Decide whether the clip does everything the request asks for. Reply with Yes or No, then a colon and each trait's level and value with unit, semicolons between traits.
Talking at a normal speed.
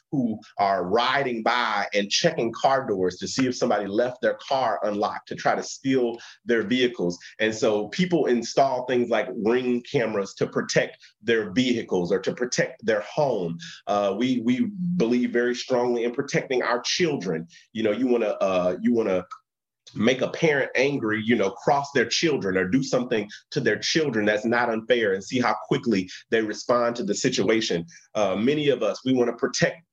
Yes: average, 185 wpm